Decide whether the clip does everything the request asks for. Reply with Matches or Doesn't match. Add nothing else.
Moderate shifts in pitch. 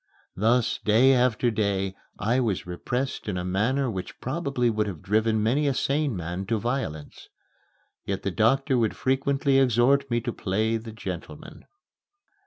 Matches